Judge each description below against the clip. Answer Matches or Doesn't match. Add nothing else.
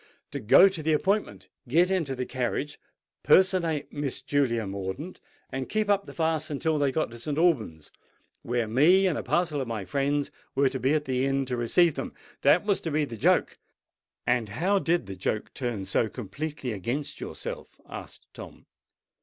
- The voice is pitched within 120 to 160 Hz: Matches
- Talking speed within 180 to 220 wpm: Matches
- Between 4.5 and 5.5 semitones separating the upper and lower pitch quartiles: Matches